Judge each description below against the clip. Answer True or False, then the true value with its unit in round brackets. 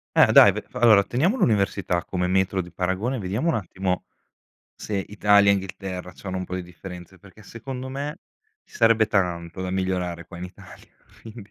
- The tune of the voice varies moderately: True (3.0 semitones)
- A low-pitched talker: True (95 Hz)